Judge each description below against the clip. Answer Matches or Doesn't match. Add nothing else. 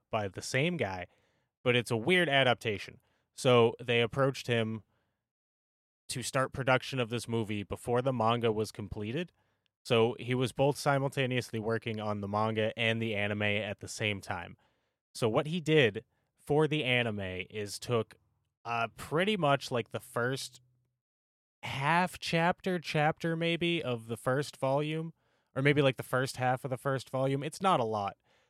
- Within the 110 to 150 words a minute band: Doesn't match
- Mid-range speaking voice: Doesn't match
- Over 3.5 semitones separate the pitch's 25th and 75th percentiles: Matches